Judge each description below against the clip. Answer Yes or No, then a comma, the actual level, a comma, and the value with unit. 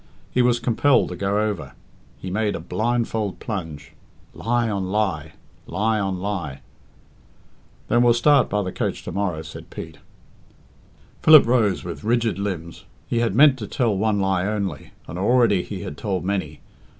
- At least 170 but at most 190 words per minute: No, average, 160 wpm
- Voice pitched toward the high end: No, low, 105 Hz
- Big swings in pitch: No, average, 4.1 semitones